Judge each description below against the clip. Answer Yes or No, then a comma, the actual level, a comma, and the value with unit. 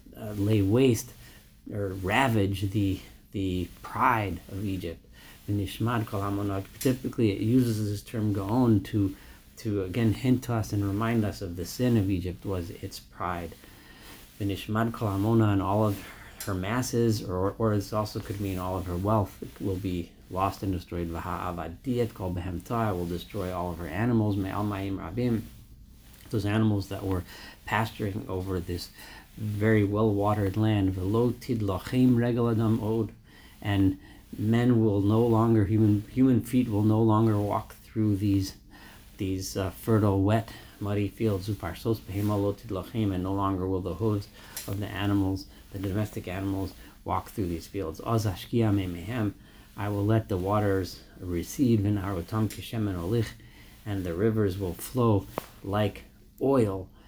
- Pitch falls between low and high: No, low, 100 Hz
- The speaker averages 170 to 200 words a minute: No, slow, 135 wpm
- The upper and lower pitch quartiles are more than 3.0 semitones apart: No, narrow, 2.4 semitones